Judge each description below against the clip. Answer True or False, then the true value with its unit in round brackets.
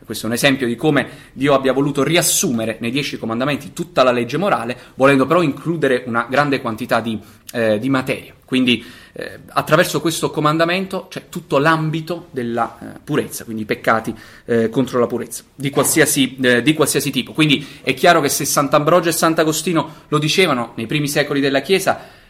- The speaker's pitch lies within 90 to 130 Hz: False (140 Hz)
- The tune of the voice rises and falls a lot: False (4.4 semitones)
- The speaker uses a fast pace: True (180 wpm)